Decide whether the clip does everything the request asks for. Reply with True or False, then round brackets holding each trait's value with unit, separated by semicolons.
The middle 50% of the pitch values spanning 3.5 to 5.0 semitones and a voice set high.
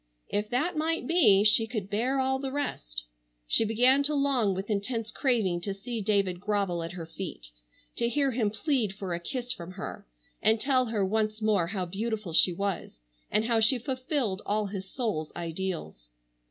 True (4.7 semitones; 215 Hz)